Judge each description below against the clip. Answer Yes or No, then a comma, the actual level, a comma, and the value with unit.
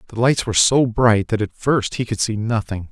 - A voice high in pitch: No, low, 110 Hz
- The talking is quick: Yes, fast, 245 wpm